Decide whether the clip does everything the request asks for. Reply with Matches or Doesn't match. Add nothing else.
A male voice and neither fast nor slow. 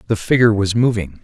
Matches